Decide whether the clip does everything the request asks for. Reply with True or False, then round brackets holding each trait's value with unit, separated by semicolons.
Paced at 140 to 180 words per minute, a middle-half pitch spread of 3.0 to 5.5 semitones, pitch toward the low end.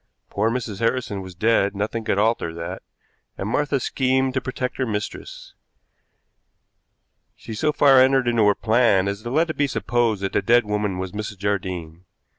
True (175 wpm; 4.2 semitones; 110 Hz)